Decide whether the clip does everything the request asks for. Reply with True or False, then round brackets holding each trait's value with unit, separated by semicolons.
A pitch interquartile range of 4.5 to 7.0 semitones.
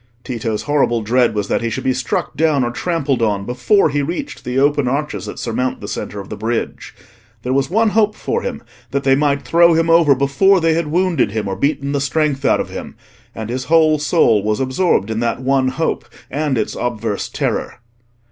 True (5.1 semitones)